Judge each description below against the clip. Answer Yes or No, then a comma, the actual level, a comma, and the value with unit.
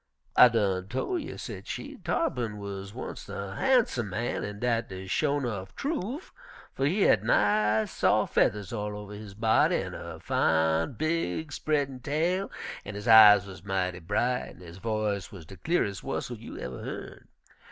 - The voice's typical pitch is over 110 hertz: No, low, 105 Hz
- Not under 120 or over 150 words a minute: No, average, 170 wpm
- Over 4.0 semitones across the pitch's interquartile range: Yes, average, 5.3 semitones